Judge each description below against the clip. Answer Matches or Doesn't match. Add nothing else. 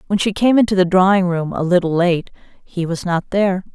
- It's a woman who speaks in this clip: Matches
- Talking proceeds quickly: Matches